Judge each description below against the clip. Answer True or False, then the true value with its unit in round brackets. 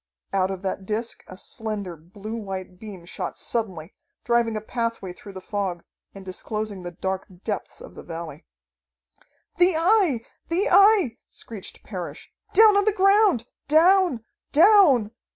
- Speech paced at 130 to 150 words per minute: True (145 wpm)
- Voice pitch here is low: False (220 Hz)